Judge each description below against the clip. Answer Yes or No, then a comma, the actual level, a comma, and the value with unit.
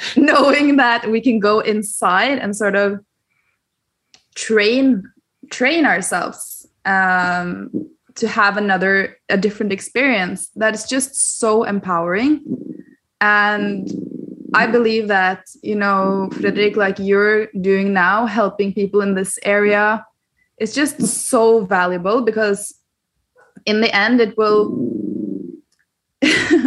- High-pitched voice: Yes, high, 215 Hz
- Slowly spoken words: Yes, slow, 110 wpm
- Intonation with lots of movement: No, average, 3.9 semitones